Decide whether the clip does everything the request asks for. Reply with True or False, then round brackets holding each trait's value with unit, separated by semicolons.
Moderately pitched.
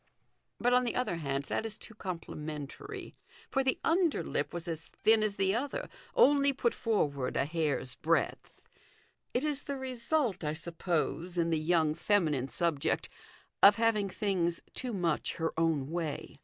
True (175 Hz)